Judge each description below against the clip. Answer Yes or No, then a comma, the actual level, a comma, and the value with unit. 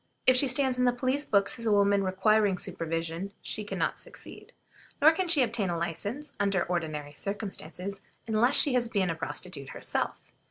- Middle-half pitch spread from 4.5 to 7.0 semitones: Yes, wide, 5.6 semitones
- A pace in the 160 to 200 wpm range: Yes, average, 185 wpm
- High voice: Yes, high, 200 Hz